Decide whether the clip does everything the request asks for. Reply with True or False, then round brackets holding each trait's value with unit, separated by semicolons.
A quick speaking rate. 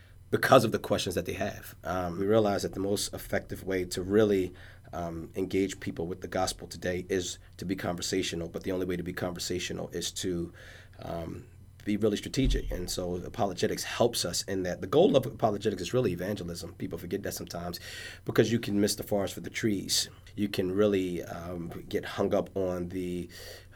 False (195 wpm)